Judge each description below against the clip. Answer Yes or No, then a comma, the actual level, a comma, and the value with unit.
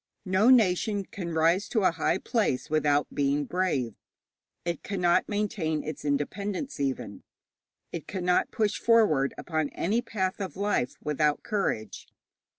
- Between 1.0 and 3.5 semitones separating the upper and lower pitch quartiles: No, wide, 5.5 semitones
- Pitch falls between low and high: Yes, medium, 175 Hz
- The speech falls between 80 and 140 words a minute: Yes, slow, 135 wpm